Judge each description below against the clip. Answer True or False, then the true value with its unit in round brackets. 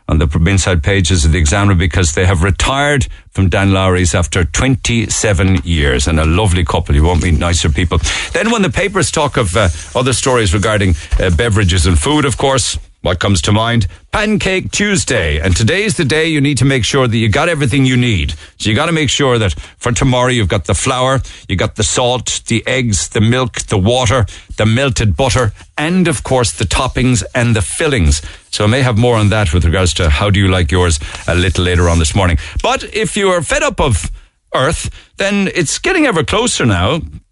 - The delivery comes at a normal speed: False (210 wpm)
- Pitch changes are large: True (6.3 semitones)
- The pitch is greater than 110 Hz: False (105 Hz)